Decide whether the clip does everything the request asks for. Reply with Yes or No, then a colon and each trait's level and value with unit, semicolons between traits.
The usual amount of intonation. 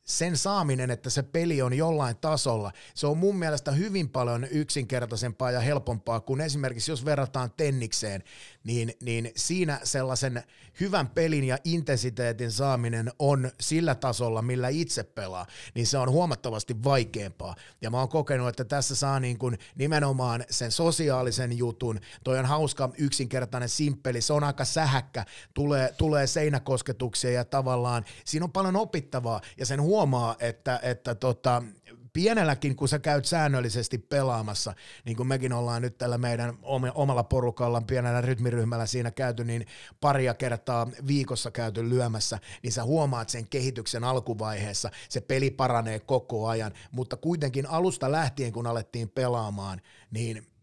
Yes: average, 3.2 semitones